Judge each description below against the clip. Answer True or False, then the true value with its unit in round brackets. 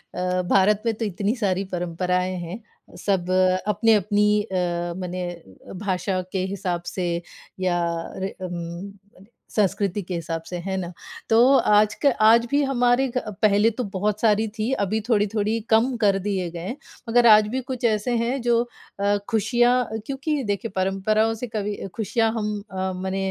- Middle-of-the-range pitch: False (205 Hz)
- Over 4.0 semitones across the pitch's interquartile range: False (3.3 semitones)